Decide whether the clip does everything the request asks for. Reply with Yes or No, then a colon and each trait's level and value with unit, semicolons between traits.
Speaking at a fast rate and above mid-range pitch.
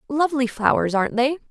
No: average, 160 wpm; very high, 260 Hz